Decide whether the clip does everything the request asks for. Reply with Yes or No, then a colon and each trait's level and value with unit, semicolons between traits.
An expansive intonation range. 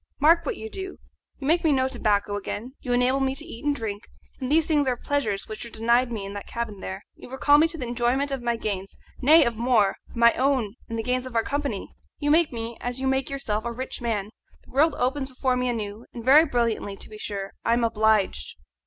No: average, 3.8 semitones